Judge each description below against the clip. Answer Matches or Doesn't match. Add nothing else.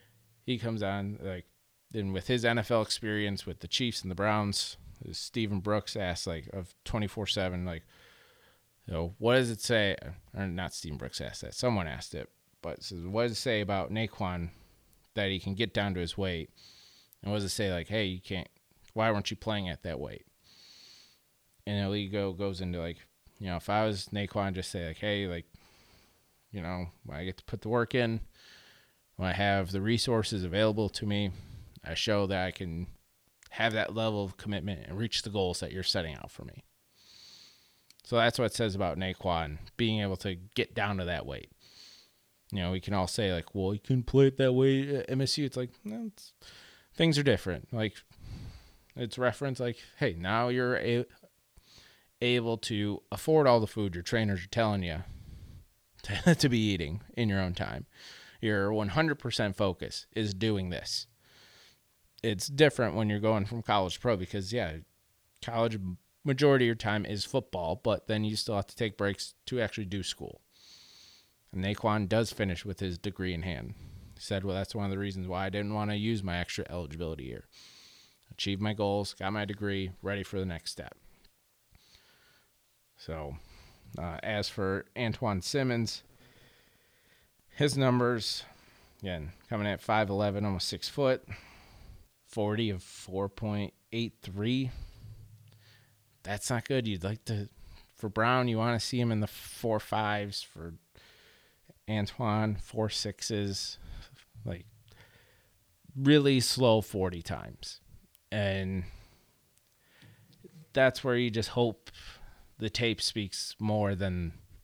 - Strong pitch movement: Doesn't match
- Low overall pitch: Matches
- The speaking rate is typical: Matches